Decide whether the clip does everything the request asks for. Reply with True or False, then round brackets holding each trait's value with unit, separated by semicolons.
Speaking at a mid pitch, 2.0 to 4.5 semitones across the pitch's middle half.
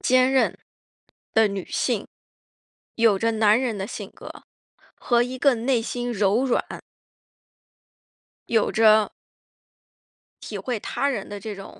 False (225 Hz; 3.0 semitones)